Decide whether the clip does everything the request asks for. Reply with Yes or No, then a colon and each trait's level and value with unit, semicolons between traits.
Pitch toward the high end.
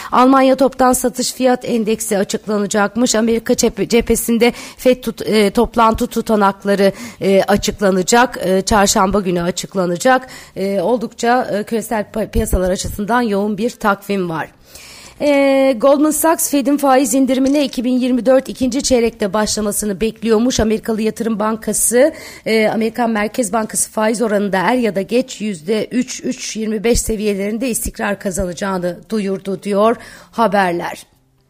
Yes: high, 220 Hz